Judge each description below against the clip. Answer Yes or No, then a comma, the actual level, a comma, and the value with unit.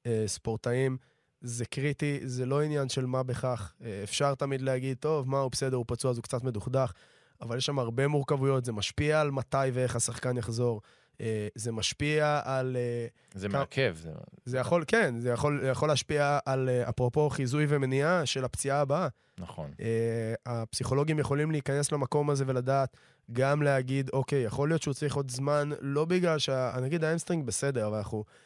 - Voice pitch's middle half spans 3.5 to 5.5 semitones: No, average, 3.1 semitones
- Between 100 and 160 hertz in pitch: Yes, low, 135 Hz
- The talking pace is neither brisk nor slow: No, fast, 160 wpm